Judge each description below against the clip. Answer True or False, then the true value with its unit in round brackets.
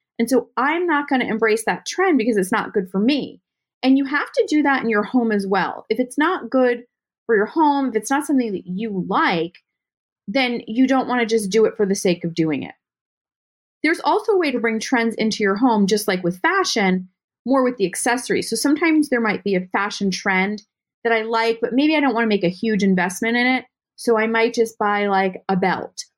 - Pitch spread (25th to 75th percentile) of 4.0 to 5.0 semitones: True (4.6 semitones)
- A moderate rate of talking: False (230 wpm)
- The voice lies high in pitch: True (230 Hz)